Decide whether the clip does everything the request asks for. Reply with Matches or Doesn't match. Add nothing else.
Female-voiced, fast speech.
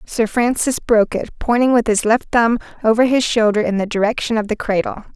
Matches